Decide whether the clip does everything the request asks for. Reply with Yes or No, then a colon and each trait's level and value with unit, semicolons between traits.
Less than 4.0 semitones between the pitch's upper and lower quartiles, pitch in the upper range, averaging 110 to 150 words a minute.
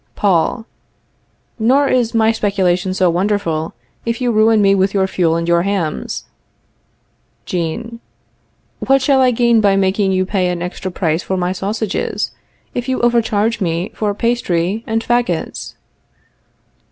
No: average, 4.3 semitones; high, 200 Hz; average, 140 wpm